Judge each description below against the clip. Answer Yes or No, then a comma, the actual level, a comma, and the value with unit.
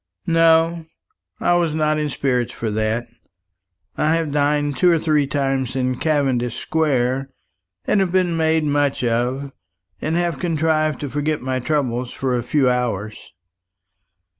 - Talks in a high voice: No, medium, 145 Hz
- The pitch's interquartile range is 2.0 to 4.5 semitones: Yes, average, 3.9 semitones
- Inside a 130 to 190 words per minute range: Yes, average, 145 wpm